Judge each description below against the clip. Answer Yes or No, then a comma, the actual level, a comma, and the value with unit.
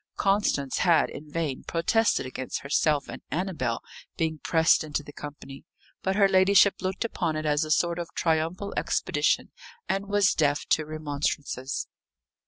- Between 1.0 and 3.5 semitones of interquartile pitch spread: No, average, 4.3 semitones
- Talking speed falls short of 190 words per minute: Yes, average, 150 wpm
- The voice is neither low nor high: Yes, medium, 160 Hz